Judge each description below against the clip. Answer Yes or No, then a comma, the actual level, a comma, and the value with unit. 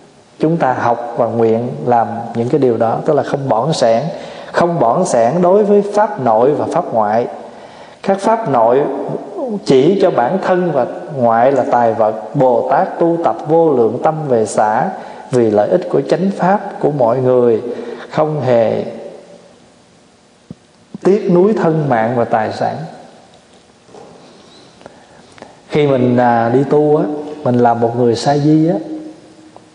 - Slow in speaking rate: Yes, slow, 155 wpm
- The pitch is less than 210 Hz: Yes, low, 135 Hz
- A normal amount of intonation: No, wide, 7.0 semitones